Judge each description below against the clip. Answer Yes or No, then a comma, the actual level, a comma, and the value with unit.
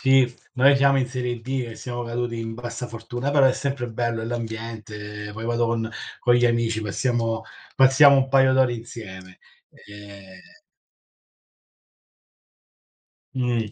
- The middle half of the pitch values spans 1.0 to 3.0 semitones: Yes, narrow, 2.4 semitones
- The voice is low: Yes, low, 120 Hz